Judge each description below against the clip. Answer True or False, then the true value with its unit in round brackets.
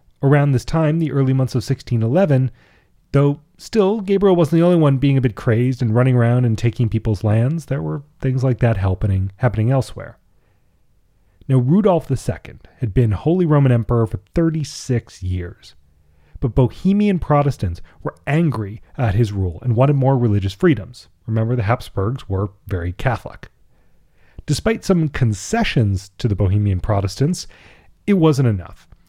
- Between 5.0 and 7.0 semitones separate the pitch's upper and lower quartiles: True (5.6 semitones)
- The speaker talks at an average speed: True (150 wpm)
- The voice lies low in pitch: True (125 Hz)